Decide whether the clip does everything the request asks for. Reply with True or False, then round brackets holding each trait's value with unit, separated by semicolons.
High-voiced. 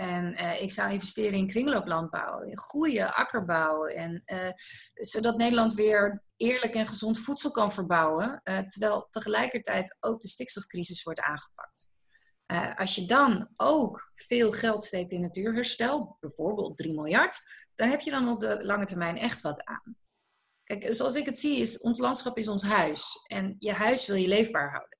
True (215 Hz)